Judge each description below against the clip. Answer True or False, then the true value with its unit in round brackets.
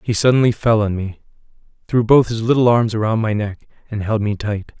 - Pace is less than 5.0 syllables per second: False (5.3 syllables/s)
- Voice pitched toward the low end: True (110 Hz)